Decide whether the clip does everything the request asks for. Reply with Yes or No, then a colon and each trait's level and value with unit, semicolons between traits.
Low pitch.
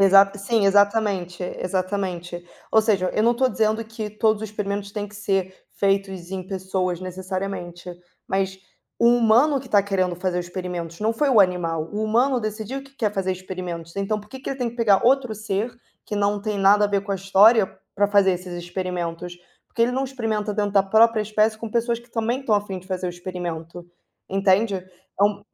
No: high, 200 Hz